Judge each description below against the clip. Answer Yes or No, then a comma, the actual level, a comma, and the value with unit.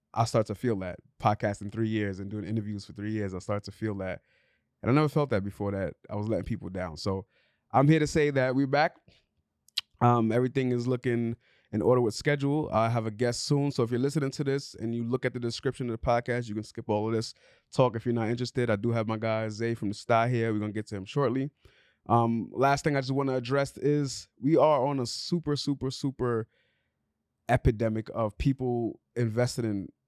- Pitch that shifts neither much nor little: Yes, average, 3.5 semitones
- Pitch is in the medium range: No, low, 115 Hz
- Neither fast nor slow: No, fast, 230 wpm